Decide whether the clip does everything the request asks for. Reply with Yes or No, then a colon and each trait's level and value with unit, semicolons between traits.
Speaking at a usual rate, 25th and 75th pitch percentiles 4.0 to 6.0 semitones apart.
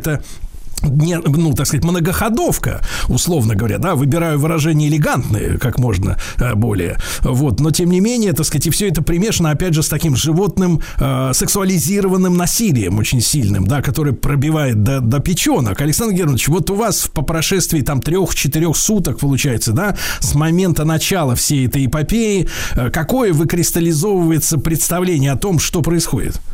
Yes: average, 150 wpm; average, 4.4 semitones